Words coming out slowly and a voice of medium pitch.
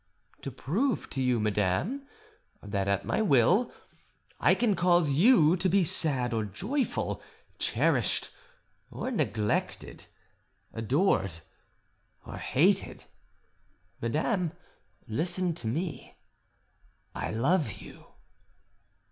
Yes: slow, 95 wpm; medium, 155 Hz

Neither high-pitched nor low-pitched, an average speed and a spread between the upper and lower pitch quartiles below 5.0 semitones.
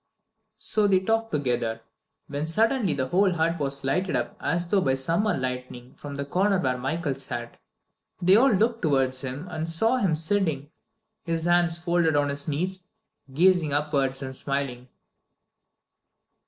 No: medium, 160 Hz; average, 155 wpm; wide, 5.4 semitones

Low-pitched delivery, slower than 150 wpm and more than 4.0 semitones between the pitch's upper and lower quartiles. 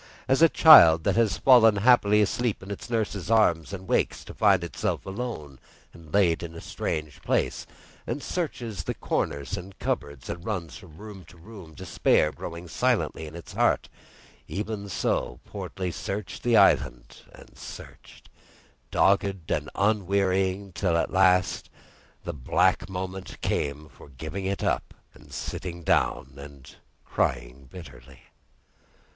Yes: very low, 95 Hz; average, 140 wpm; average, 4.4 semitones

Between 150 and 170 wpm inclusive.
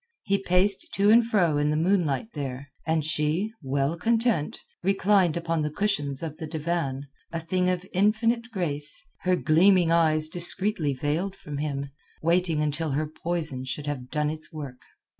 Yes: average, 160 wpm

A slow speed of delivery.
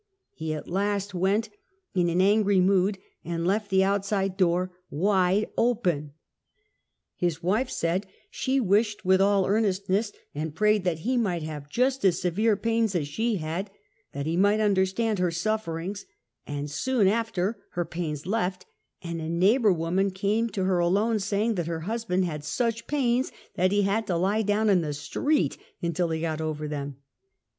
No: average, 170 wpm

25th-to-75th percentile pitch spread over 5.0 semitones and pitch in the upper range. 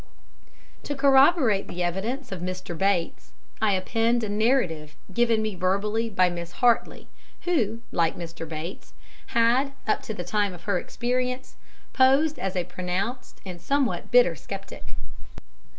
Yes: wide, 5.5 semitones; high, 210 Hz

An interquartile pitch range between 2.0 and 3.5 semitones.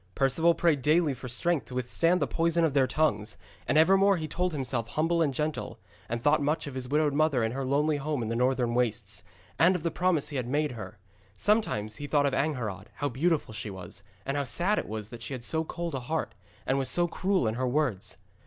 No: average, 4.9 semitones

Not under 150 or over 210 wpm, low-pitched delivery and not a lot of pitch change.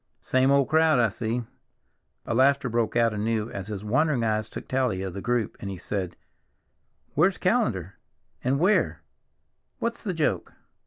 No: average, 160 wpm; low, 120 Hz; average, 4.8 semitones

